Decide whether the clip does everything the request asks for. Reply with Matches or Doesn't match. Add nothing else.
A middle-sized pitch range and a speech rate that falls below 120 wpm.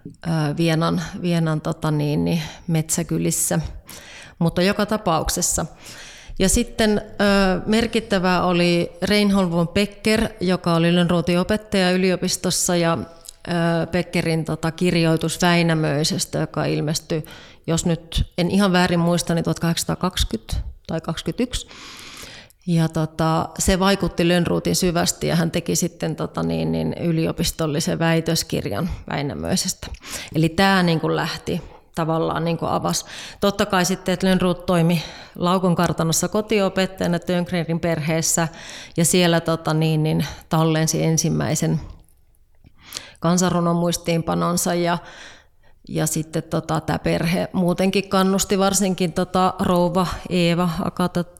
Doesn't match